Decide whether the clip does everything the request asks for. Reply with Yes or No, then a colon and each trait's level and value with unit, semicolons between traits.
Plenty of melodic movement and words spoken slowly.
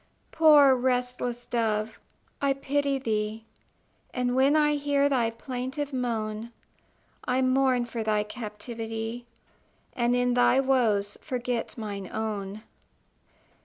No: average, 3.1 semitones; slow, 110 wpm